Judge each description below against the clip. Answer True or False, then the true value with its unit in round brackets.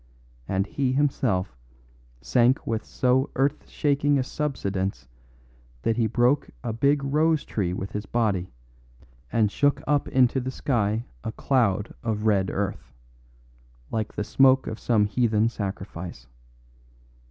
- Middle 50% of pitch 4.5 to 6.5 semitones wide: True (4.8 semitones)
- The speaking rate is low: True (130 wpm)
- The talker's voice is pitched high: False (115 Hz)